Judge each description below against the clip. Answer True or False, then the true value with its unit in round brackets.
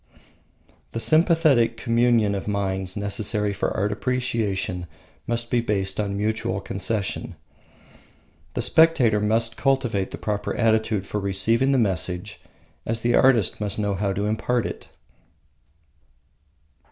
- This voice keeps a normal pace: False (125 wpm)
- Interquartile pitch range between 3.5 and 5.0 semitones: False (2.9 semitones)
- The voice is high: False (105 Hz)